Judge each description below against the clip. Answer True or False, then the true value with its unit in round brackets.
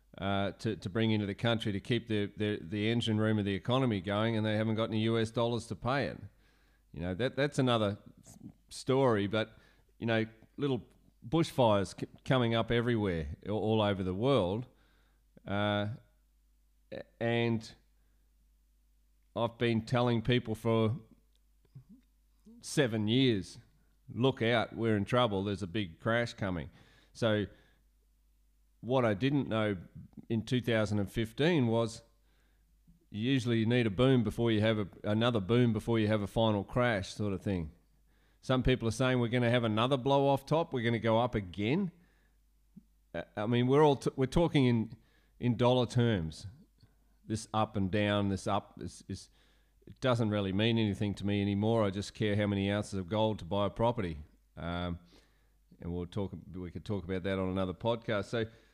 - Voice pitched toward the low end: True (110 Hz)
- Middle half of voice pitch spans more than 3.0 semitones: True (3.4 semitones)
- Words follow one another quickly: False (170 wpm)